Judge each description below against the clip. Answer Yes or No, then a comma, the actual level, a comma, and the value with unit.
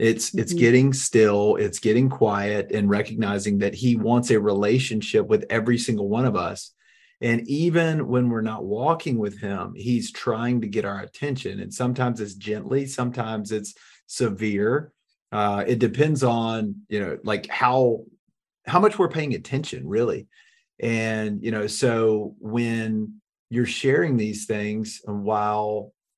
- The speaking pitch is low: Yes, low, 115 Hz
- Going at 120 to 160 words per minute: Yes, average, 150 wpm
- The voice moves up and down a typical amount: Yes, average, 3.2 semitones